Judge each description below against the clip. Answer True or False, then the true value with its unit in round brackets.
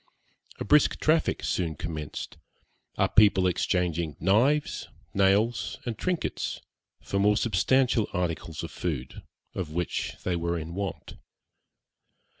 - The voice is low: True (95 Hz)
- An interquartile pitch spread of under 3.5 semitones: False (4.8 semitones)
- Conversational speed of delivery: False (115 wpm)